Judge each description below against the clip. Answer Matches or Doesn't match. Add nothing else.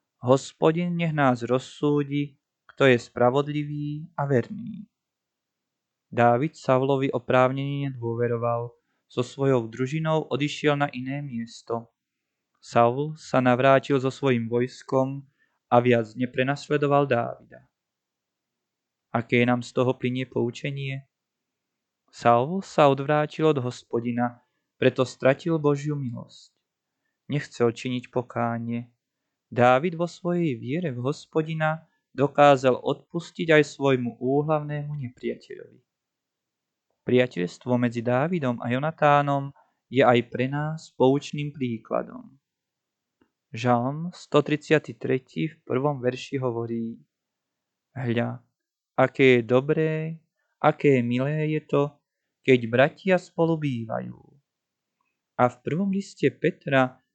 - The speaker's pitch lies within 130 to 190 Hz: Matches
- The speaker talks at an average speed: Doesn't match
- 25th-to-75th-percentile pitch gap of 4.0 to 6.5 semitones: Doesn't match